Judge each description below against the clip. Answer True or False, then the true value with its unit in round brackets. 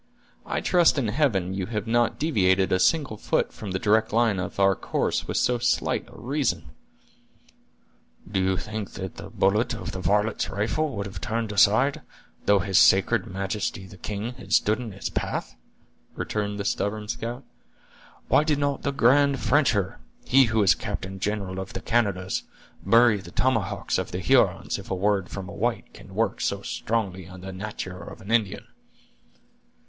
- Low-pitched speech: True (105 Hz)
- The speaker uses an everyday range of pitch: True (3.7 semitones)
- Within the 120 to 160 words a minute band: False (175 wpm)